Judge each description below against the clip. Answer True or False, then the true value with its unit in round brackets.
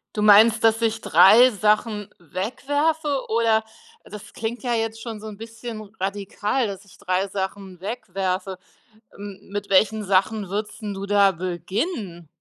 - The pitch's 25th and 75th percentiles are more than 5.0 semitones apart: False (2.6 semitones)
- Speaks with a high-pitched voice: True (210 Hz)